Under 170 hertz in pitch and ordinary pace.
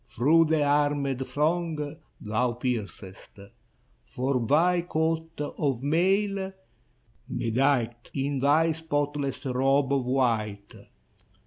No: medium, 140 Hz; slow, 95 wpm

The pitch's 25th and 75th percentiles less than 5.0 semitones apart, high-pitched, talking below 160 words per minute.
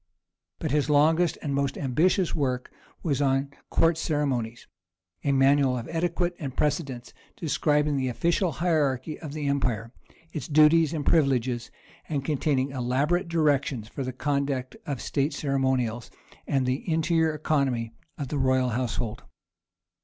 No: average, 3.1 semitones; medium, 140 Hz; average, 140 wpm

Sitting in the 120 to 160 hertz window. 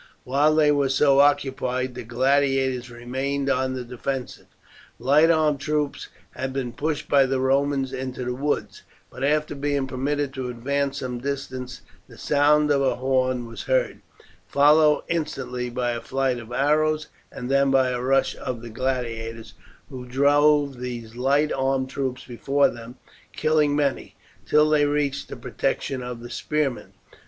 Yes: low, 135 Hz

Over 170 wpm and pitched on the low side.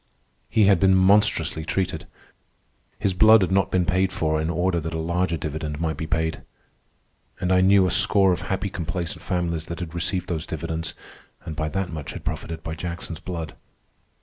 Yes: average, 185 wpm; very low, 85 Hz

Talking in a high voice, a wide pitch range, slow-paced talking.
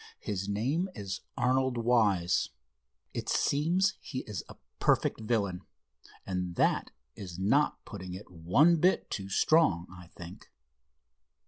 No: low, 105 Hz; wide, 6.4 semitones; slow, 125 wpm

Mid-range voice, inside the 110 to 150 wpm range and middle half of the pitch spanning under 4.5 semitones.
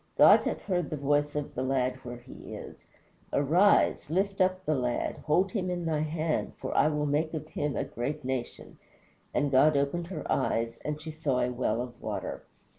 No: medium, 150 Hz; average, 195 wpm; average, 3.8 semitones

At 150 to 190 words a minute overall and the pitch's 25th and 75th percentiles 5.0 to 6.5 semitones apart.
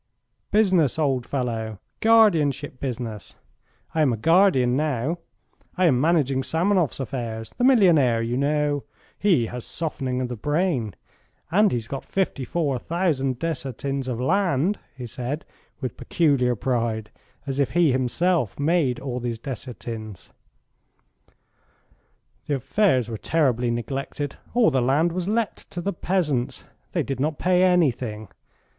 No: average, 140 wpm; wide, 5.5 semitones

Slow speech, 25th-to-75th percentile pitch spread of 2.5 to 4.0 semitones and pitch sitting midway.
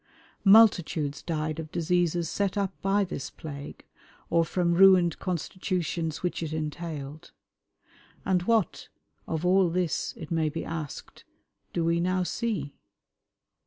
Yes: slow, 125 wpm; average, 2.8 semitones; medium, 170 Hz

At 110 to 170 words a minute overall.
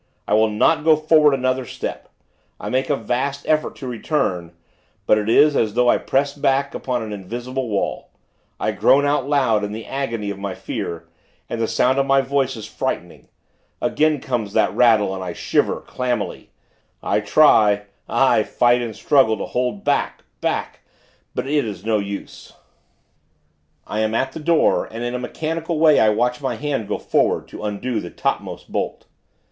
No: average, 180 wpm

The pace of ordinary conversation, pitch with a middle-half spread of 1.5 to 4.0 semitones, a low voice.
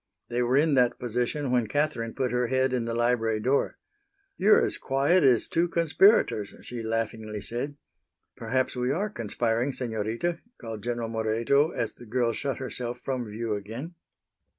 Yes: average, 160 wpm; average, 3.2 semitones; low, 125 Hz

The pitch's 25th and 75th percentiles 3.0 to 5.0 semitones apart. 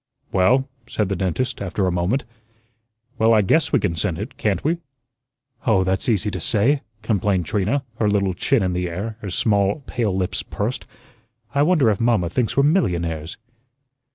Yes: average, 4.7 semitones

